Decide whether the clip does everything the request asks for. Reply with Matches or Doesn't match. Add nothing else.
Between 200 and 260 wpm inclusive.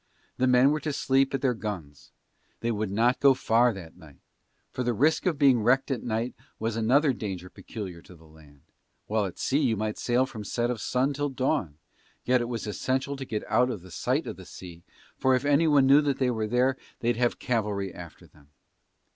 Matches